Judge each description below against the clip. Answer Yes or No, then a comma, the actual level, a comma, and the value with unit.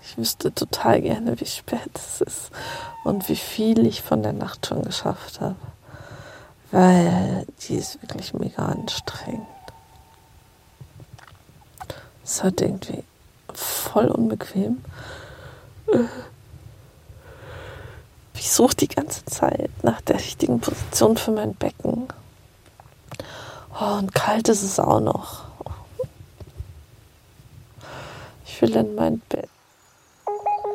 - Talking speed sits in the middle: No, slow, 105 wpm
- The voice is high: Yes, high, 210 Hz